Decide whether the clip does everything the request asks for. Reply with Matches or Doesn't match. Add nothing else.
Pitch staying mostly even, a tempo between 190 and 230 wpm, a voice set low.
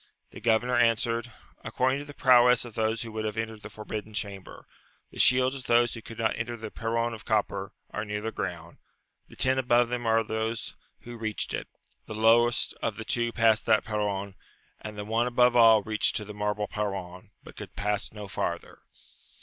Matches